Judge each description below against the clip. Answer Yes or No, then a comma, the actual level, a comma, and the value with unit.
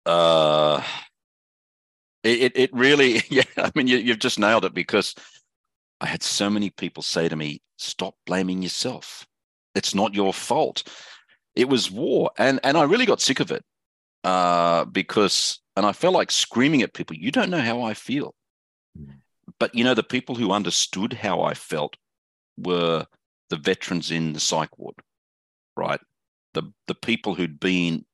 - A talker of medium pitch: No, very low, 90 Hz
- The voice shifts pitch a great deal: Yes, wide, 6.0 semitones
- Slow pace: No, average, 165 wpm